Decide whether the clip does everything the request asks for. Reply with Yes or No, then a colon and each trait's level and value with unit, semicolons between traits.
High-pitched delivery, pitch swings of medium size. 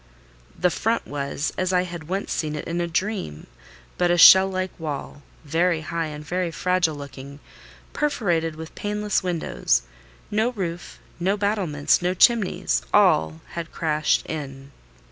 No: medium, 170 Hz; average, 3.6 semitones